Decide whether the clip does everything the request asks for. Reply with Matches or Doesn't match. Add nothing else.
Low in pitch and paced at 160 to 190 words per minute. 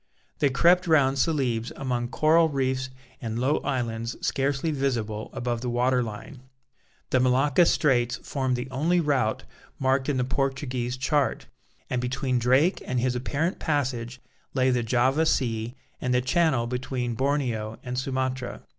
Doesn't match